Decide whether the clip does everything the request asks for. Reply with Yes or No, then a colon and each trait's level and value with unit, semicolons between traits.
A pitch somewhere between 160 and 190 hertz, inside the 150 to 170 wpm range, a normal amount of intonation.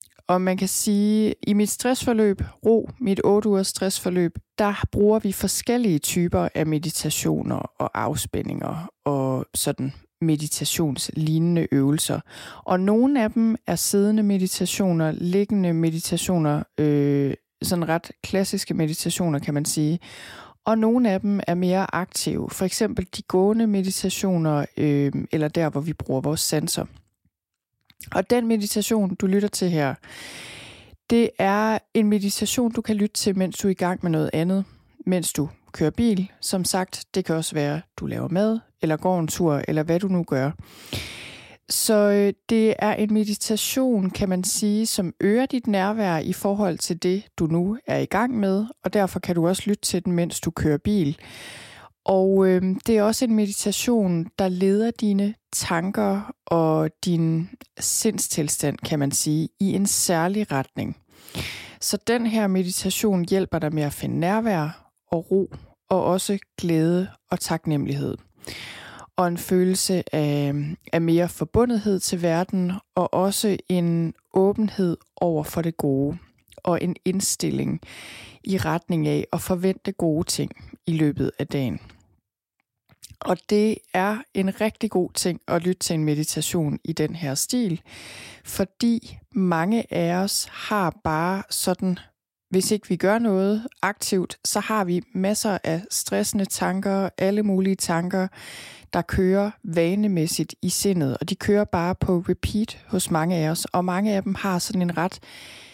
Yes: medium, 185 Hz; average, 155 wpm; average, 3.9 semitones